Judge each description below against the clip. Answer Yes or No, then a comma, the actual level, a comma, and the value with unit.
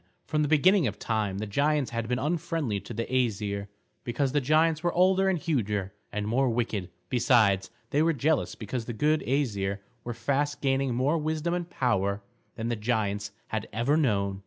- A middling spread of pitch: No, wide, 6.1 semitones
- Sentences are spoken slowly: No, average, 180 wpm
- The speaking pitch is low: Yes, low, 125 Hz